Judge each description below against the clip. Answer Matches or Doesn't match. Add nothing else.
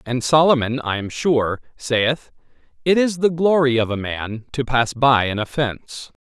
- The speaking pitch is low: Matches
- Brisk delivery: Doesn't match